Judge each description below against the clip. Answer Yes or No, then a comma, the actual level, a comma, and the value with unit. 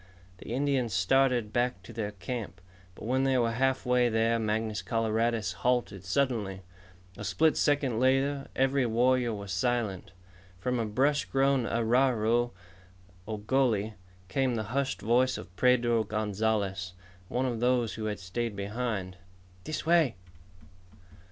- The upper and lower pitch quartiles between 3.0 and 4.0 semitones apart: Yes, average, 3.3 semitones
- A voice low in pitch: Yes, low, 115 Hz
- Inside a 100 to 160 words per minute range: Yes, slow, 135 wpm